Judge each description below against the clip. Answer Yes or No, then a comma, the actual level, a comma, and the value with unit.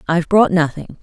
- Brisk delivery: No, average, 175 wpm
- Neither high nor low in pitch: Yes, medium, 175 Hz